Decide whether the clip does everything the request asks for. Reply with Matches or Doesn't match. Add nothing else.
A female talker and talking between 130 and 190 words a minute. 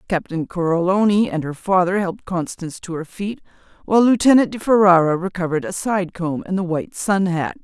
Matches